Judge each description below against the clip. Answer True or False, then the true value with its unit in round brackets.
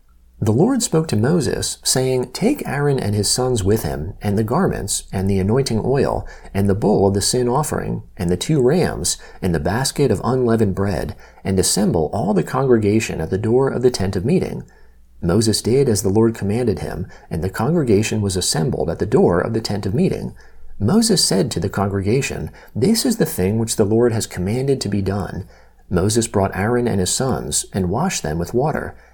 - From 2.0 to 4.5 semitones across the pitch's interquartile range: False (4.9 semitones)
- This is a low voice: True (110 Hz)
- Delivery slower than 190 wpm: False (200 wpm)